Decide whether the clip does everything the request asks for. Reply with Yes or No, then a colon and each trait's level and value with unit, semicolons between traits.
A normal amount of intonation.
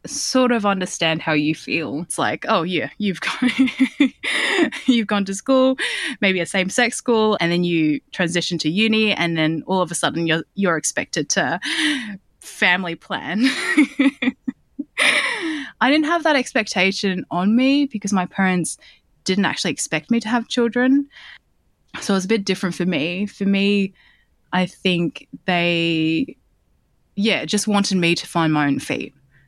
No: wide, 6.3 semitones